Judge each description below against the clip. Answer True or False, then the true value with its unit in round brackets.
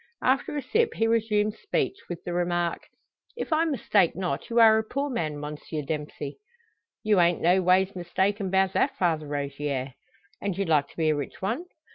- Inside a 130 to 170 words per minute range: False (185 wpm)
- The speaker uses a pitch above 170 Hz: True (185 Hz)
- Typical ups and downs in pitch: False (5.9 semitones)